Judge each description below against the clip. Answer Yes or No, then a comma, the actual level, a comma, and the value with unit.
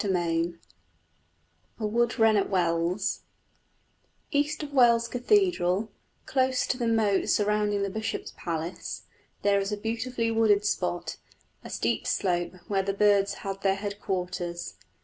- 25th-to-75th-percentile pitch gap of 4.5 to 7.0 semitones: No, average, 3.5 semitones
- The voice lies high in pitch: Yes, high, 205 Hz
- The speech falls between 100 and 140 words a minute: Yes, slow, 135 wpm